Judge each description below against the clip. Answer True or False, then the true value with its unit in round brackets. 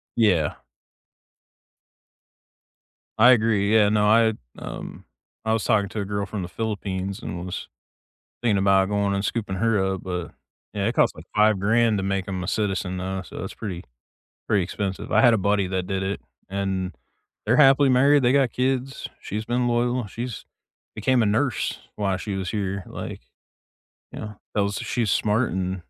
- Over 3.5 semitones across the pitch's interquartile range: False (3.1 semitones)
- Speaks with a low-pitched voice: True (105 Hz)